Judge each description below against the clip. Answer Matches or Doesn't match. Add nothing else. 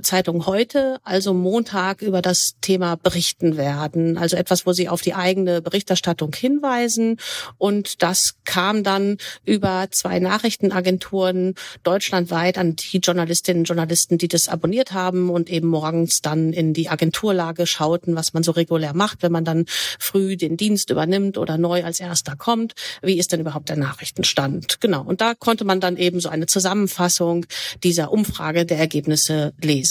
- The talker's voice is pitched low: Doesn't match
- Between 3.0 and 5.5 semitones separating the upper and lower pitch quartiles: Doesn't match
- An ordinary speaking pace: Matches